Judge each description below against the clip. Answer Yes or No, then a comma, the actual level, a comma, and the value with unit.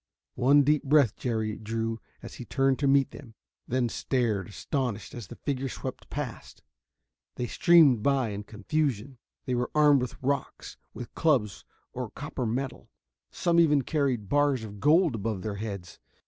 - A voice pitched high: No, low, 125 Hz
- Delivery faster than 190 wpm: No, average, 160 wpm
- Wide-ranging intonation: No, average, 4.3 semitones